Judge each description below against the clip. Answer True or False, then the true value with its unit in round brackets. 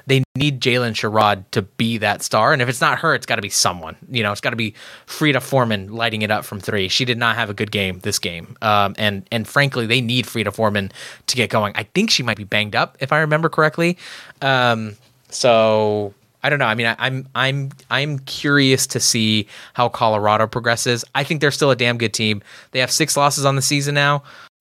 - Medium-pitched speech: False (120 Hz)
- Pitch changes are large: False (4.2 semitones)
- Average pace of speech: False (230 wpm)